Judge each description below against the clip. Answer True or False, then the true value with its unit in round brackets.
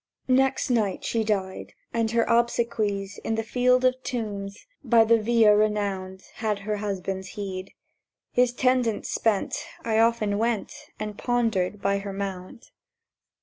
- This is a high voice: True (215 Hz)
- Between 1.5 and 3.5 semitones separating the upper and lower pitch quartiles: True (2.9 semitones)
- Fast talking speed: False (140 wpm)